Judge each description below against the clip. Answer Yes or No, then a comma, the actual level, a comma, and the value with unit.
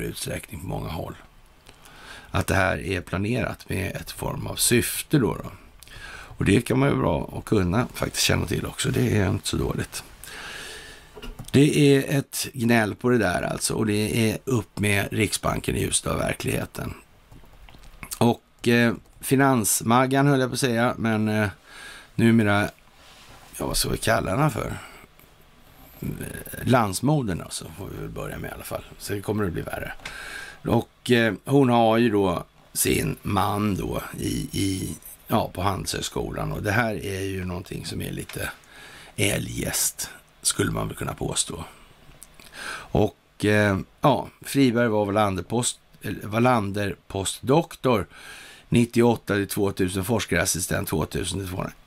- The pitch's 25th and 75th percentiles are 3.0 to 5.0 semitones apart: Yes, average, 3.9 semitones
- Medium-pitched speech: No, low, 110 Hz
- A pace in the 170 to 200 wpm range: No, average, 150 wpm